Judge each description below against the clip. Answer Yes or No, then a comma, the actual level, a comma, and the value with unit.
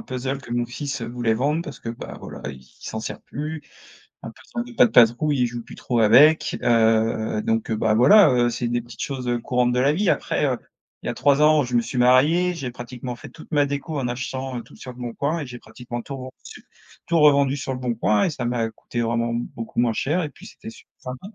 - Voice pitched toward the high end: No, low, 125 Hz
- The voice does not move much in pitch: No, average, 3.2 semitones